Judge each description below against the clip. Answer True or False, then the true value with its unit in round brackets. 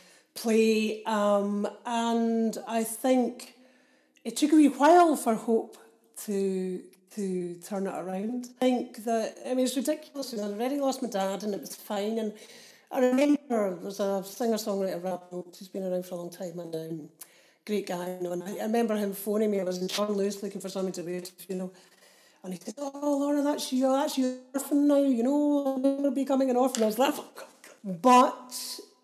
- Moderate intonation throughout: True (5.0 semitones)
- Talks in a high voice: True (220 Hz)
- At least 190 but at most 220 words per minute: True (200 wpm)